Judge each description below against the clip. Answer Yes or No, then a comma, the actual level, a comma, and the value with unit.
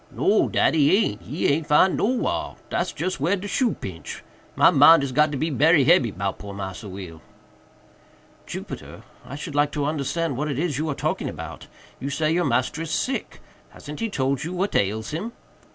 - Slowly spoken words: No, average, 185 wpm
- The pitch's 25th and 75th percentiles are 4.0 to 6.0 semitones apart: Yes, average, 4.5 semitones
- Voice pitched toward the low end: No, medium, 150 Hz